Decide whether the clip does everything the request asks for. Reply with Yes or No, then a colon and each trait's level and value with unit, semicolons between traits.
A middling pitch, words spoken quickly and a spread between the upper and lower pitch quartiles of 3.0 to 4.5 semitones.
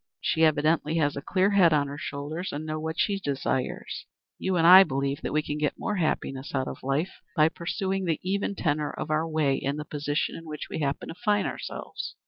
Yes: medium, 155 Hz; fast, 220 wpm; average, 3.3 semitones